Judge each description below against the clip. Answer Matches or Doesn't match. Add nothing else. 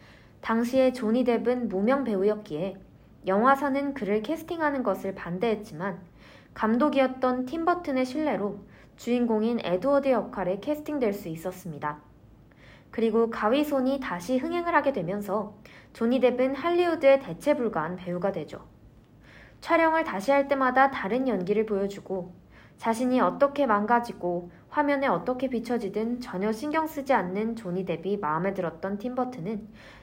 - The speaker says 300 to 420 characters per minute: Matches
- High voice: Matches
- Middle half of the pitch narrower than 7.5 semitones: Matches